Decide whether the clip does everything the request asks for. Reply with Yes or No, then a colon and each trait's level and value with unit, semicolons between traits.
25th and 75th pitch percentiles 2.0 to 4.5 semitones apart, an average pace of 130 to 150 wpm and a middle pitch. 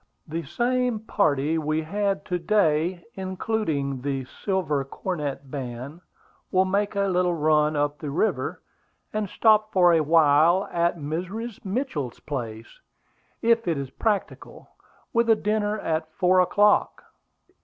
No: wide, 5.6 semitones; slow, 135 wpm; medium, 170 Hz